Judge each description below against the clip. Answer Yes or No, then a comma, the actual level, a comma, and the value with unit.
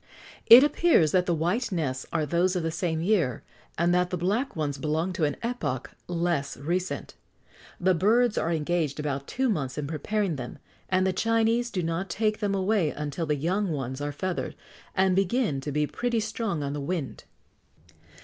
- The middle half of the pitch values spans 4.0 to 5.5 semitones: Yes, average, 5.2 semitones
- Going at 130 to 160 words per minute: No, average, 185 wpm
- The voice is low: No, medium, 175 Hz